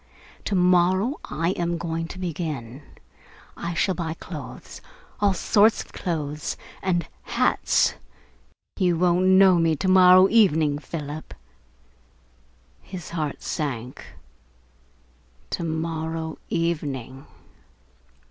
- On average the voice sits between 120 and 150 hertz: No, medium, 170 Hz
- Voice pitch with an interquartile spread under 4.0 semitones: Yes, average, 2.9 semitones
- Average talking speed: No, slow, 100 wpm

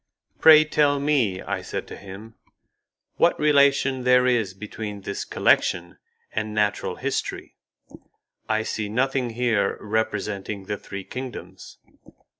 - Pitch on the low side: Yes, low, 110 Hz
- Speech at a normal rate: No, slow, 120 wpm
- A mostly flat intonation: No, average, 4.4 semitones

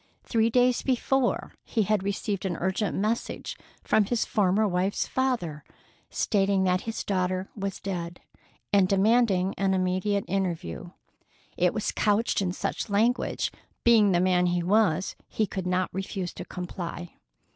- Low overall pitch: No, high, 195 Hz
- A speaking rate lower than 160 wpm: Yes, average, 145 wpm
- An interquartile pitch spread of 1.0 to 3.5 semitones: Yes, average, 2.9 semitones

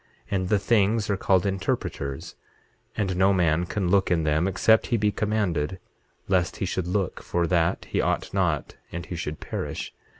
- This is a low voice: Yes, very low, 95 Hz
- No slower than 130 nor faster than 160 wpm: No, average, 175 wpm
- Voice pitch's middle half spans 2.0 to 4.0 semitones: Yes, average, 2.7 semitones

